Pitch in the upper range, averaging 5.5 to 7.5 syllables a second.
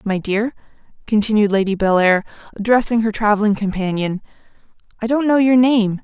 Yes: high, 215 Hz; 5.6 syllables/s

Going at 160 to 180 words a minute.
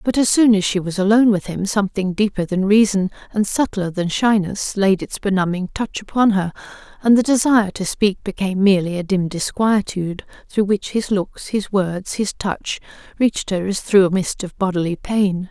No: average, 195 wpm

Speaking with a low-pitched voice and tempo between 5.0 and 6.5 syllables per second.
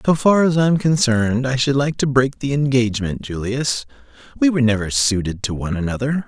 Yes: low, 125 Hz; 5.8 syllables/s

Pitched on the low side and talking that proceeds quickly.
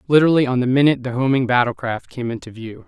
Yes: low, 130 Hz; fast, 210 wpm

